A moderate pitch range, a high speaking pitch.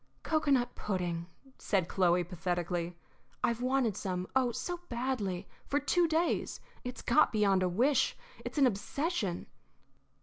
No: wide, 6.8 semitones; high, 215 Hz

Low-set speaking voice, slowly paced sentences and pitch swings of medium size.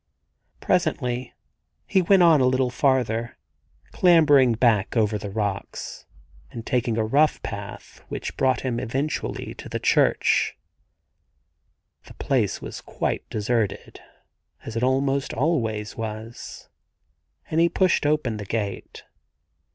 Yes: low, 125 Hz; slow, 120 wpm; average, 4.4 semitones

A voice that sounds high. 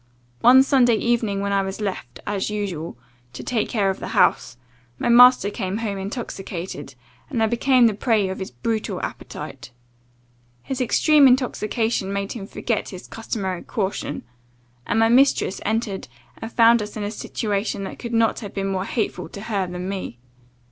Yes: high, 210 Hz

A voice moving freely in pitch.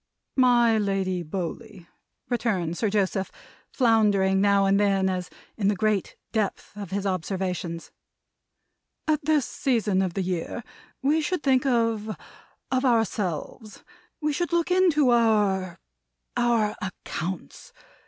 No: average, 3.9 semitones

